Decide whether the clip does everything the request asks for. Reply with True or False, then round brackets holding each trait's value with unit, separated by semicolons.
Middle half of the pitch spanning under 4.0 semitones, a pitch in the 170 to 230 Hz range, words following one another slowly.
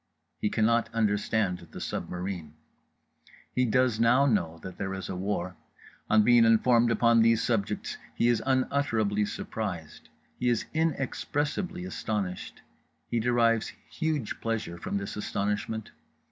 False (3.3 semitones; 110 Hz; 130 wpm)